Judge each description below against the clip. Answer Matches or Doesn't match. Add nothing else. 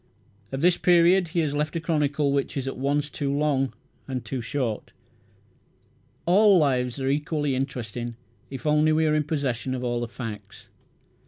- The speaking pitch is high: Doesn't match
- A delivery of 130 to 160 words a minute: Doesn't match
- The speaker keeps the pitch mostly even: Doesn't match